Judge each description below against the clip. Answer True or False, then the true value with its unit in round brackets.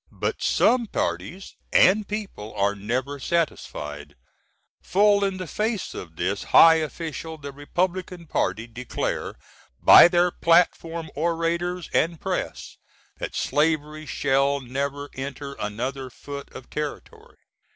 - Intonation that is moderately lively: True (4.9 semitones)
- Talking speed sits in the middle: False (120 wpm)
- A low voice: False (150 Hz)